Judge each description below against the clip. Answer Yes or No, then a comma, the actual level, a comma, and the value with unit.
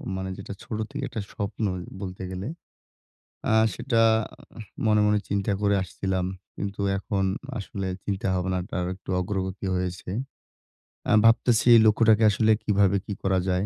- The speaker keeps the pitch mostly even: Yes, narrow, 2.1 semitones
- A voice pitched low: Yes, low, 100 Hz